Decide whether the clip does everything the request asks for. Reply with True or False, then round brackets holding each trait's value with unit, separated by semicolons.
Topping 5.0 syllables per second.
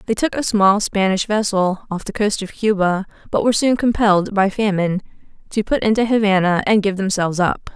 True (5.6 syllables/s)